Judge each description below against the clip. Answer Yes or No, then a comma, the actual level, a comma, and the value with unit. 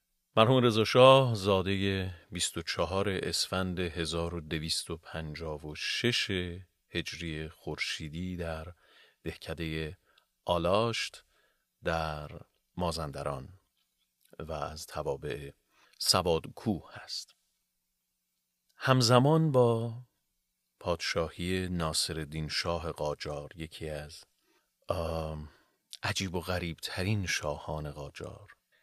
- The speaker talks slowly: Yes, slow, 65 wpm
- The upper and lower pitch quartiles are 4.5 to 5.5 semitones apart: No, average, 3.7 semitones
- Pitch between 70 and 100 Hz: Yes, very low, 85 Hz